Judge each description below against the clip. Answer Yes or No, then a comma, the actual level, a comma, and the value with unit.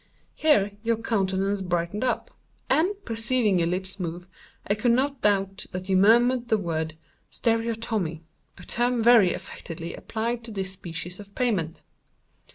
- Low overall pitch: No, high, 205 Hz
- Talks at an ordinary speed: Yes, average, 145 wpm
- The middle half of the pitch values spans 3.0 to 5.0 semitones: Yes, average, 4.3 semitones